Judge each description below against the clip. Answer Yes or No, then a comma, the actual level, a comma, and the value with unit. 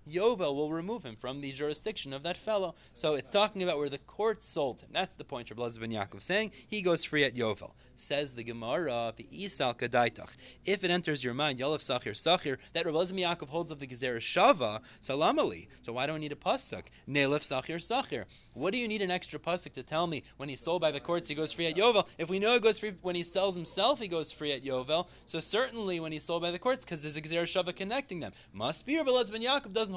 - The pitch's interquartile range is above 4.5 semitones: Yes, average, 5.1 semitones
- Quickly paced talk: Yes, fast, 235 wpm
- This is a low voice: No, medium, 165 Hz